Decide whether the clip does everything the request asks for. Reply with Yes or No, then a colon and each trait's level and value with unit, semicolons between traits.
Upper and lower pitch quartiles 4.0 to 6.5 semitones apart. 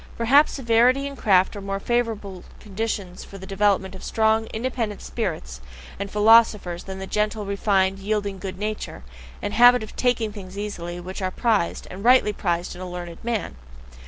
No: average, 3.0 semitones